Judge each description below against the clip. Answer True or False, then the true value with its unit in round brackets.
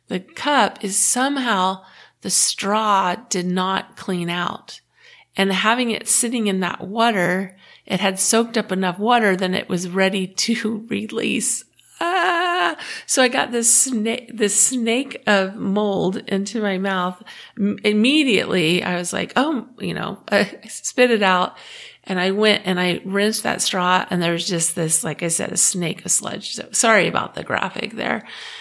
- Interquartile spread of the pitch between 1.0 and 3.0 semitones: False (4.0 semitones)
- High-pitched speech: True (200 Hz)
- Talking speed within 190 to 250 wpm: False (165 wpm)